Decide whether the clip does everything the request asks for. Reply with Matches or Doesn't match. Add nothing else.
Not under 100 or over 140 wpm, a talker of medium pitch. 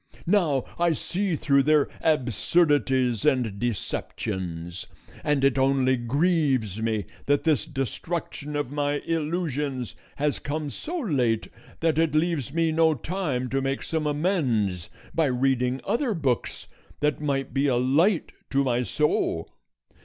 Matches